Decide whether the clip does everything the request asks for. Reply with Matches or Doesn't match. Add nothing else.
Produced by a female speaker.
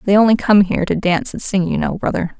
Matches